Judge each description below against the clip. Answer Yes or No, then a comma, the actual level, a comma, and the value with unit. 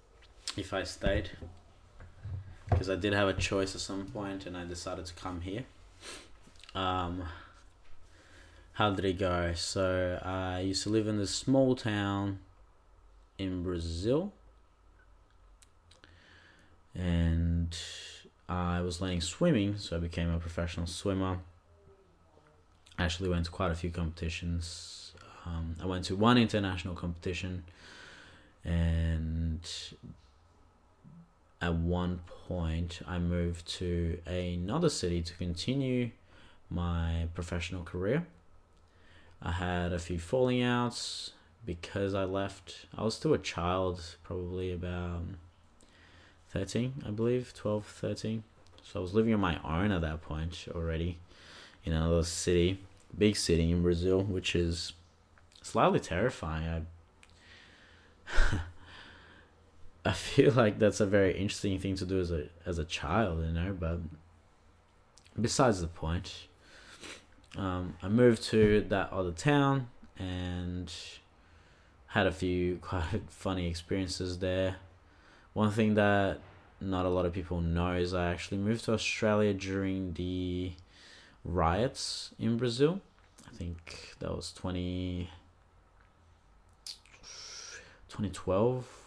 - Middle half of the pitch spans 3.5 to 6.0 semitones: No, narrow, 2.4 semitones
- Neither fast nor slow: No, slow, 120 wpm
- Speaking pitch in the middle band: No, very low, 90 Hz